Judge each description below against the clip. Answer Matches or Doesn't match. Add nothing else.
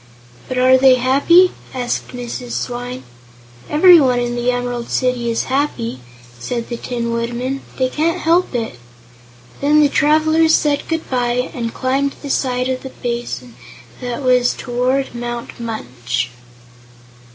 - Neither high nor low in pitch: Doesn't match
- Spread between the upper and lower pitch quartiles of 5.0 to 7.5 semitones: Doesn't match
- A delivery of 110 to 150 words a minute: Matches